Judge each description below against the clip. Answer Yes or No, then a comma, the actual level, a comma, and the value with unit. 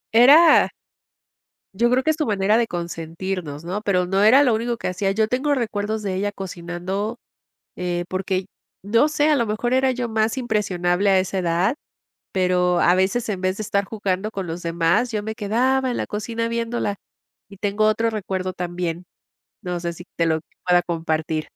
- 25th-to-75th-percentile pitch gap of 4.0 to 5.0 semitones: Yes, average, 4.3 semitones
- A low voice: No, high, 200 Hz